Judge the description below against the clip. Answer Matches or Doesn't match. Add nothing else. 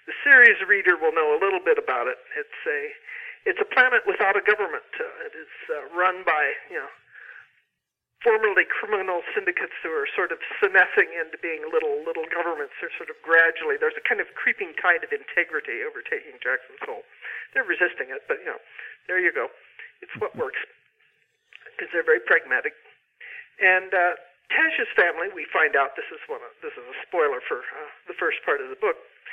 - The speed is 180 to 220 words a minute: Matches